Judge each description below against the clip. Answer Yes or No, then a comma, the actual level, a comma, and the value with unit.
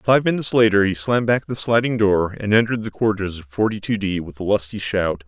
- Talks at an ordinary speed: No, fast, 240 wpm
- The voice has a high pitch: No, low, 105 Hz